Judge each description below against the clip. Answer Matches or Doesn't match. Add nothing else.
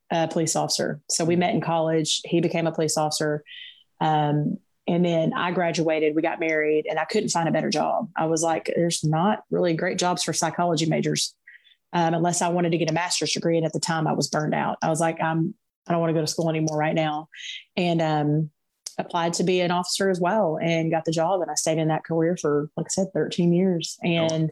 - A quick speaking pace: Matches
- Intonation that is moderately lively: Doesn't match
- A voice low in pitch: Doesn't match